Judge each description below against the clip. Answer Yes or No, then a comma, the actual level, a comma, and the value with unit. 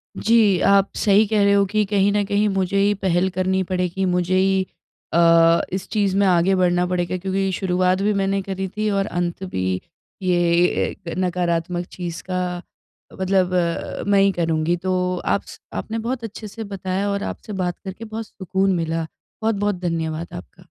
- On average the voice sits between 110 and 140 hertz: No, high, 190 Hz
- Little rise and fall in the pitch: Yes, narrow, 2.1 semitones